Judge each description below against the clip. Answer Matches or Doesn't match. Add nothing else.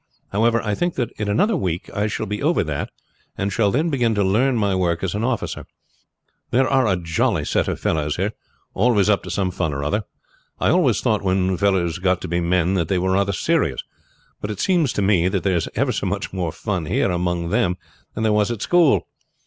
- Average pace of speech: Doesn't match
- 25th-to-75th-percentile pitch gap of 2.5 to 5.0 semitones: Matches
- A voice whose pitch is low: Matches